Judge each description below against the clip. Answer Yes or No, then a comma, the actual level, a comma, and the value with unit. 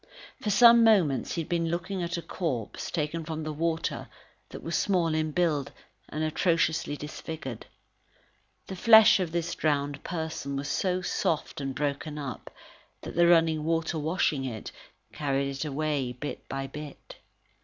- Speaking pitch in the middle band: Yes, medium, 155 Hz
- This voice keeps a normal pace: Yes, average, 155 wpm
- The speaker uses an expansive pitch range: No, average, 2.9 semitones